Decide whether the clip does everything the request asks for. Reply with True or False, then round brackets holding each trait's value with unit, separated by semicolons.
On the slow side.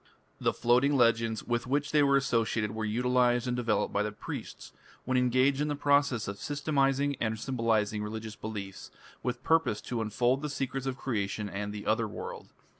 False (175 wpm)